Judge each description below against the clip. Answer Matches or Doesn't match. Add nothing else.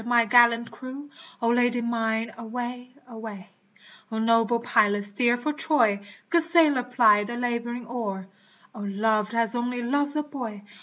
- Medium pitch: Doesn't match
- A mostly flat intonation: Matches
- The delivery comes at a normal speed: Matches